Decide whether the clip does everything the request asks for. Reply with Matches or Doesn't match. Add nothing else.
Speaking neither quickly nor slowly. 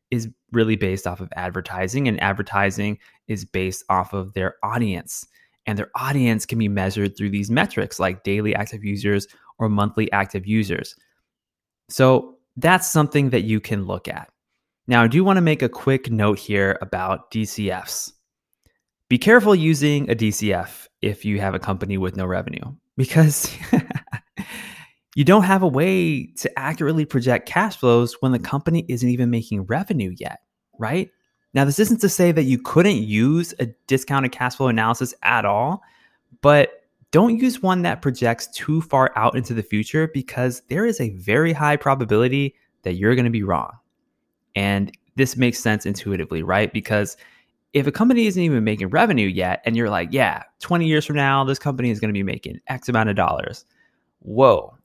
Matches